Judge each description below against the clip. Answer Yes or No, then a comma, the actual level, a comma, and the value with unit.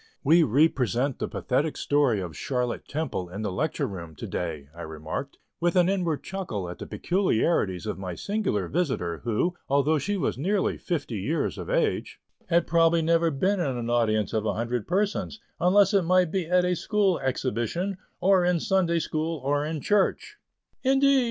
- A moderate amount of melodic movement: No, wide, 7.7 semitones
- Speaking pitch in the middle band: Yes, medium, 155 Hz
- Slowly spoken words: No, average, 175 wpm